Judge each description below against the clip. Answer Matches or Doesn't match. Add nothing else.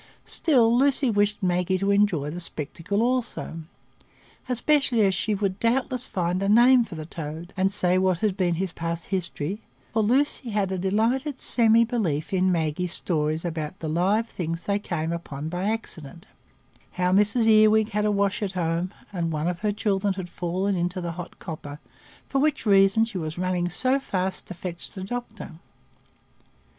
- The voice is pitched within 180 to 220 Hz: Matches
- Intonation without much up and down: Doesn't match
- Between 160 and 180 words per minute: Matches